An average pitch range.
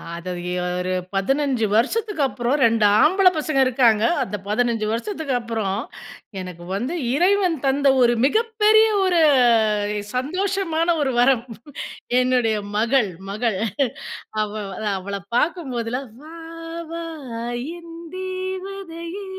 No: wide, 7.8 semitones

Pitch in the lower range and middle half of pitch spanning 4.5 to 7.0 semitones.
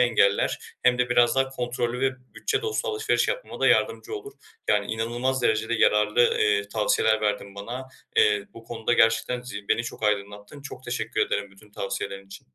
No: low, 115 Hz; average, 3.7 semitones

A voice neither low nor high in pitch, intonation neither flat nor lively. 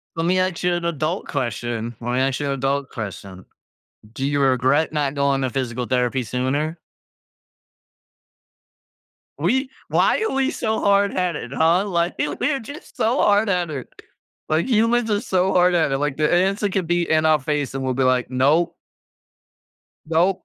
No: medium, 155 Hz; wide, 5.7 semitones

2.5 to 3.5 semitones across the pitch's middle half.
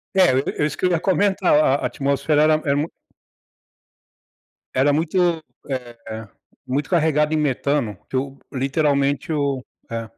Yes: average, 2.9 semitones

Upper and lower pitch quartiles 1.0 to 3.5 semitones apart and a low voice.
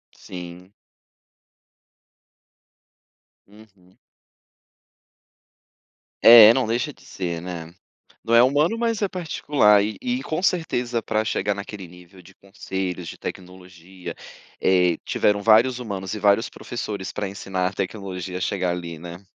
No: average, 4.2 semitones; low, 100 Hz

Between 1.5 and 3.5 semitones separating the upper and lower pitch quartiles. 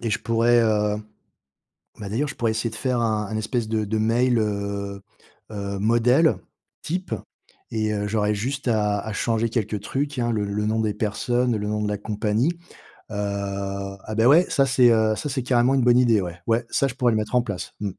Yes: average, 2.7 semitones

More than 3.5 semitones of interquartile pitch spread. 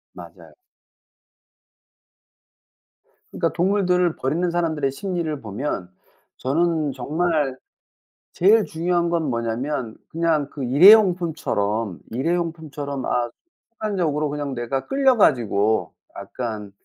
Yes: average, 5.2 semitones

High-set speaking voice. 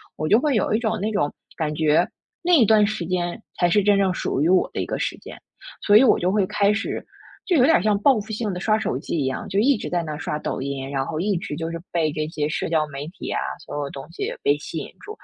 No: medium, 180 Hz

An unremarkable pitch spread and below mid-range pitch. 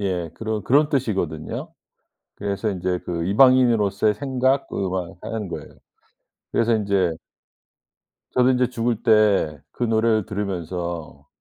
Yes: average, 4.3 semitones; low, 105 Hz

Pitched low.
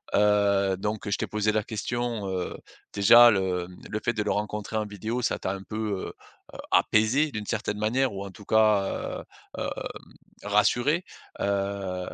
Yes: low, 105 Hz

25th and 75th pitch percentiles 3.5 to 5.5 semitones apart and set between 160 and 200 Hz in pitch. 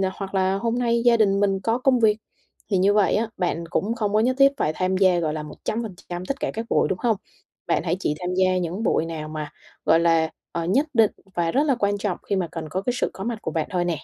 Yes: average, 4.5 semitones; high, 195 Hz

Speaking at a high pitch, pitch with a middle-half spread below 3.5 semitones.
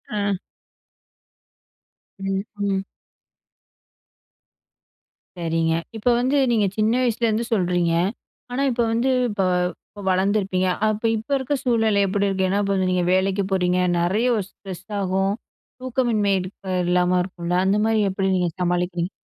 Yes: high, 195 Hz; average, 3.1 semitones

